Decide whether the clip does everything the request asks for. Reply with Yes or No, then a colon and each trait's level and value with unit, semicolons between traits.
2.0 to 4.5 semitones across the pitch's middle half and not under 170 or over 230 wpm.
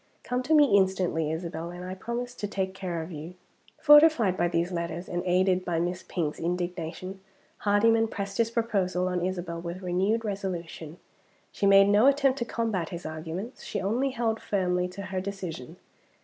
Yes: average, 3.6 semitones; average, 175 wpm